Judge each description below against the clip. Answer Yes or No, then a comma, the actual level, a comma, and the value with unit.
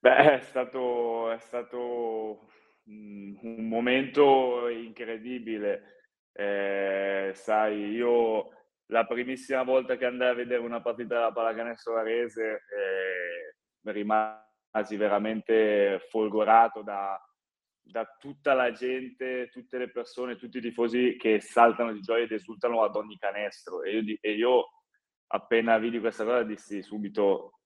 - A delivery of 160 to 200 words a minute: No, average, 125 wpm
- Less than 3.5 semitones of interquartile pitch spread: Yes, narrow, 2.5 semitones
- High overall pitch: No, low, 115 Hz